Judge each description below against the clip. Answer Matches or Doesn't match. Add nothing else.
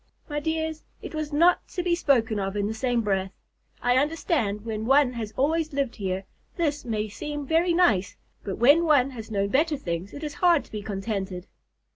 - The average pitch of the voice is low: Doesn't match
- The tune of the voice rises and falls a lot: Matches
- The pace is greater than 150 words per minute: Matches